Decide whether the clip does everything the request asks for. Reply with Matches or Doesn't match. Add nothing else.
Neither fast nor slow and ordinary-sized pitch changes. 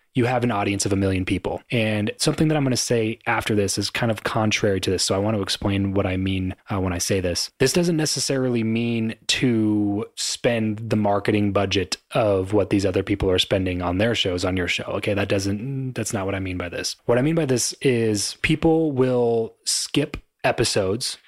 Doesn't match